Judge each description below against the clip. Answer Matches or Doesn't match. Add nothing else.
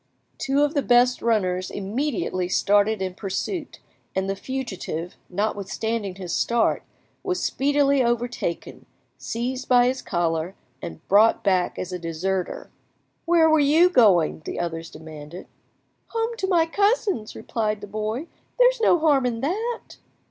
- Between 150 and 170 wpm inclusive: Doesn't match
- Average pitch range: Doesn't match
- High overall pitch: Matches